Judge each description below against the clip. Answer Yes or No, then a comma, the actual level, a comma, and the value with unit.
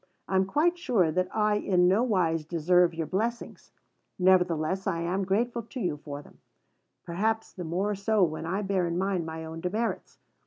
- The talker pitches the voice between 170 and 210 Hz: Yes, medium, 185 Hz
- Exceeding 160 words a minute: Yes, average, 185 wpm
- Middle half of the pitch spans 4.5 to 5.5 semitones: No, average, 3.7 semitones